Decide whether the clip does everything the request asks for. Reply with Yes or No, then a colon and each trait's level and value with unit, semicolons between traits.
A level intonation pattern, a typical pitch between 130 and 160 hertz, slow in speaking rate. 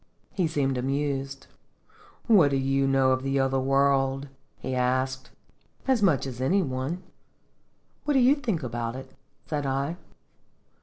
No: narrow, 2.3 semitones; low, 135 Hz; average, 145 wpm